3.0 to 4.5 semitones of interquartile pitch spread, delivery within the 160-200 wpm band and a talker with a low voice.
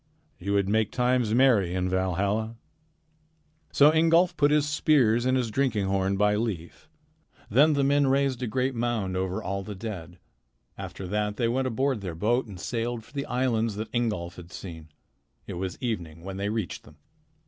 No: average, 5.1 semitones; average, 180 wpm; low, 110 Hz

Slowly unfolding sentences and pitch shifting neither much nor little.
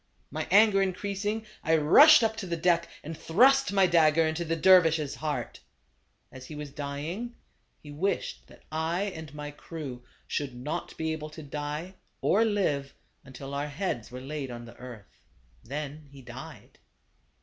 No: average, 160 wpm; average, 4.6 semitones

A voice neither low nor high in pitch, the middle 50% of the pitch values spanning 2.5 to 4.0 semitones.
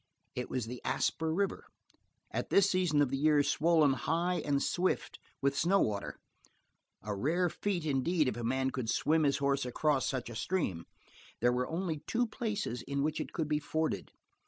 No: medium, 150 Hz; average, 4.7 semitones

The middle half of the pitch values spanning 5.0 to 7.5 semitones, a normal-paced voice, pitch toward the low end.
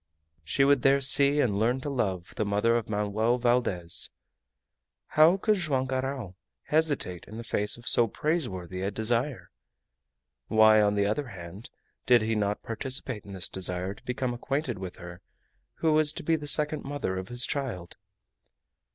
Yes: wide, 5.4 semitones; average, 170 wpm; low, 120 Hz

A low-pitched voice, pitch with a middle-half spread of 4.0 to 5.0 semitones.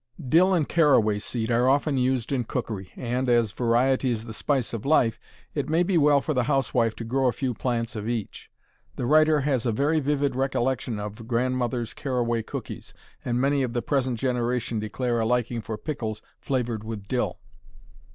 No: low, 125 Hz; average, 2.9 semitones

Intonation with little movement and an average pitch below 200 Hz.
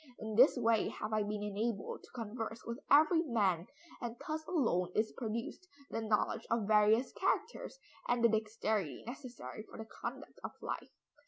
No: narrow, 2.3 semitones; high, 225 Hz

